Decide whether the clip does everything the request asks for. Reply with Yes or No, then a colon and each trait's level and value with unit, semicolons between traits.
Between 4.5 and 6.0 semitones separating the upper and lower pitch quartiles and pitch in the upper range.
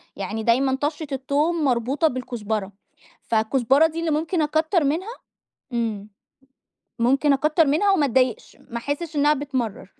Yes: average, 4.8 semitones; very high, 275 Hz